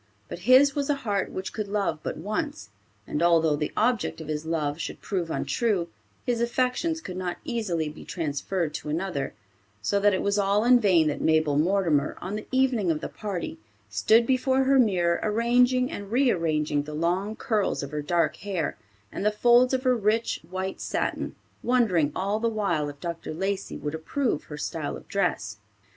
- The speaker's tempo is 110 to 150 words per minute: No, average, 185 wpm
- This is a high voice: Yes, high, 195 Hz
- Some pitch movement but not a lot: No, wide, 6.5 semitones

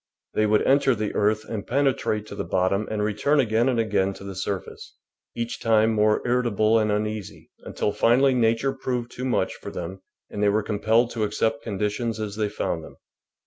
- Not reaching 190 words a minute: No, average, 195 wpm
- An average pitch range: No, narrow, 2.3 semitones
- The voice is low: Yes, low, 110 Hz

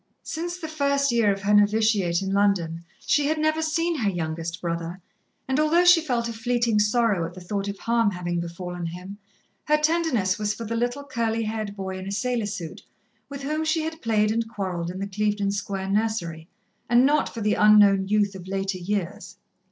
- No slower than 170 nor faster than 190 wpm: No, average, 200 wpm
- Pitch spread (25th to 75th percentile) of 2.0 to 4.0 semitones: No, average, 4.5 semitones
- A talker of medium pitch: No, high, 210 Hz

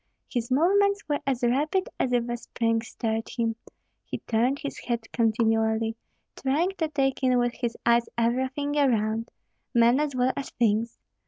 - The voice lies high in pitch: Yes, high, 245 Hz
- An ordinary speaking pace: Yes, average, 160 wpm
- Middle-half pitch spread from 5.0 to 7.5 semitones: No, average, 3.3 semitones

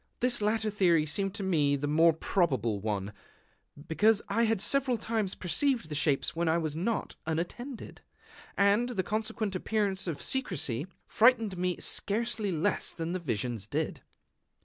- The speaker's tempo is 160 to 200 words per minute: No, average, 150 wpm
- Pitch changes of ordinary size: No, wide, 5.7 semitones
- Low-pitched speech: No, medium, 185 Hz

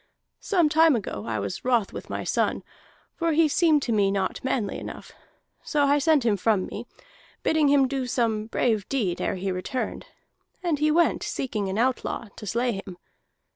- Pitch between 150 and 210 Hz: No, high, 245 Hz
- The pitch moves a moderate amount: No, wide, 6.5 semitones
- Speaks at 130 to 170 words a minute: No, average, 180 wpm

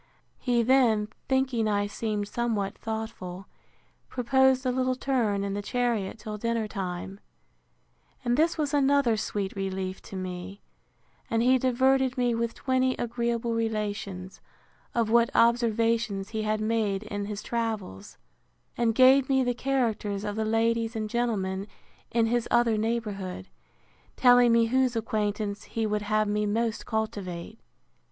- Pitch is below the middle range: No, high, 225 Hz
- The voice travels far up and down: No, average, 2.8 semitones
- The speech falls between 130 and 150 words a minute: Yes, average, 140 wpm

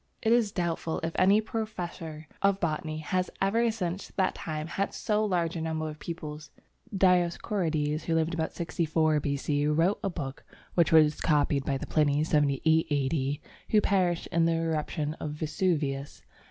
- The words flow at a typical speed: Yes, average, 160 wpm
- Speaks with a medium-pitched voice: Yes, medium, 160 Hz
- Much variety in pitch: No, average, 3.2 semitones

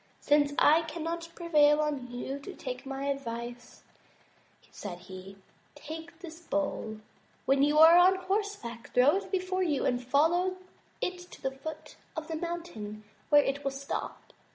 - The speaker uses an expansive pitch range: No, average, 4.4 semitones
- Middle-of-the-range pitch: No, very high, 295 Hz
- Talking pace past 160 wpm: No, average, 155 wpm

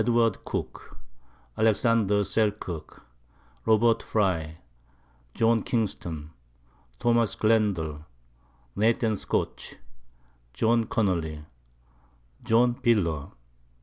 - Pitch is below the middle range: Yes, low, 105 Hz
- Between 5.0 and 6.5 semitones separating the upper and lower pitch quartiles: Yes, wide, 5.4 semitones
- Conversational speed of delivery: No, slow, 65 wpm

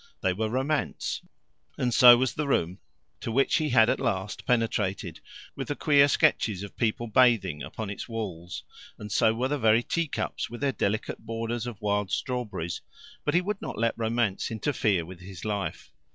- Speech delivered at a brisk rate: No, average, 180 wpm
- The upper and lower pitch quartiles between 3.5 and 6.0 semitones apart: Yes, average, 3.9 semitones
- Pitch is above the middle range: No, low, 115 Hz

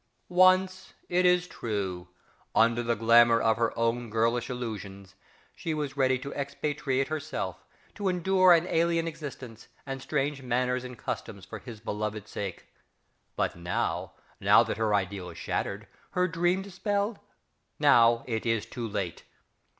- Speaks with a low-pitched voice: Yes, low, 125 Hz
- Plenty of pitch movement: Yes, wide, 6.8 semitones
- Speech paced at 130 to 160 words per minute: Yes, average, 150 wpm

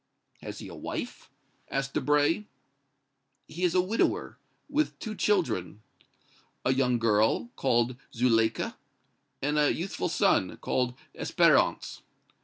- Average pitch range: No, wide, 7.2 semitones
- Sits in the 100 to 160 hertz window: Yes, low, 135 Hz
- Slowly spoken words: Yes, slow, 115 wpm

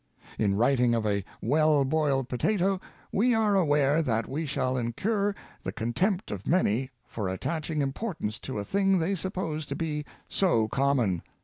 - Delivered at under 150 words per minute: No, average, 165 wpm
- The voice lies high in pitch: No, medium, 145 Hz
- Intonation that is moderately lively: No, wide, 7.5 semitones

